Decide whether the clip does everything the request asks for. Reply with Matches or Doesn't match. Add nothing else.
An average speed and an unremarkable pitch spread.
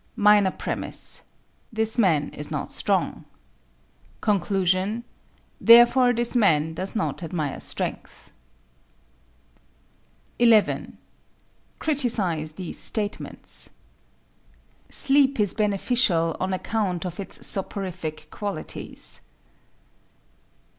Doesn't match